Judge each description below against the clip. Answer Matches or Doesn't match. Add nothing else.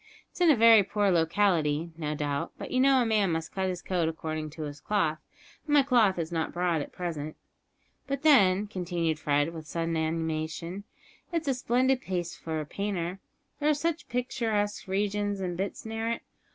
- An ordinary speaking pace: Matches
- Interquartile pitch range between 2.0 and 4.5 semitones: Doesn't match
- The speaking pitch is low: Doesn't match